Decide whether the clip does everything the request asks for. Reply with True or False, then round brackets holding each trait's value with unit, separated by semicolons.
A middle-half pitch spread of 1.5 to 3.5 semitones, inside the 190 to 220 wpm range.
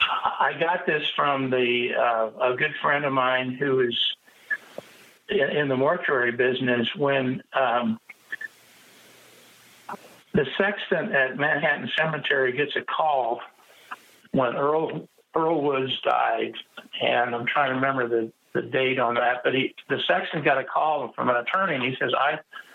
False (2.9 semitones; 150 wpm)